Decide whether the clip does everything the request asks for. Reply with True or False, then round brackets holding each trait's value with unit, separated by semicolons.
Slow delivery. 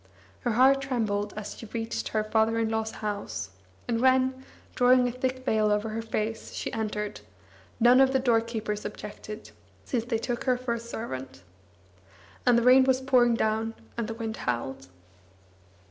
False (165 wpm)